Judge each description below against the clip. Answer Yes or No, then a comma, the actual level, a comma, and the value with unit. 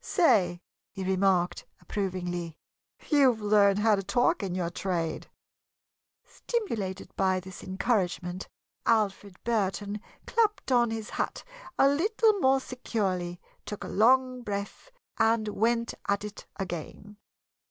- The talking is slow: Yes, slow, 120 wpm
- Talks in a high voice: Yes, high, 205 Hz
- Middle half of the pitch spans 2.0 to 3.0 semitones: No, average, 4.0 semitones